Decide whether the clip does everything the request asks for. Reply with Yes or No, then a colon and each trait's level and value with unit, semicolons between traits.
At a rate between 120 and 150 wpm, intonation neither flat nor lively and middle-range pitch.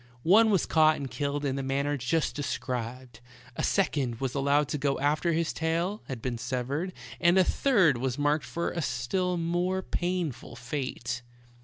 No: average, 170 wpm; average, 4.6 semitones; medium, 145 Hz